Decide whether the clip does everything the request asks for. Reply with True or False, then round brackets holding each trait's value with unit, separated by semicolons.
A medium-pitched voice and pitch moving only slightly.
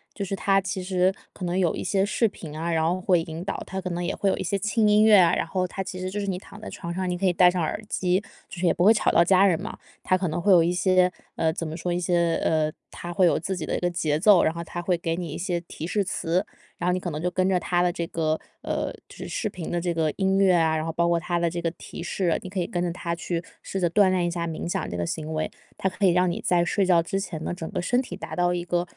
True (175 Hz; 1.9 semitones)